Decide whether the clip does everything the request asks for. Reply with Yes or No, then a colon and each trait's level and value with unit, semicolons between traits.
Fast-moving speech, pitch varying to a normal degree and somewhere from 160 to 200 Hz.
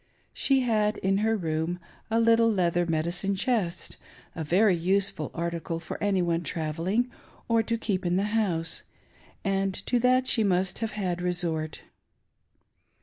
No: average, 155 wpm; average, 4.4 semitones; high, 190 Hz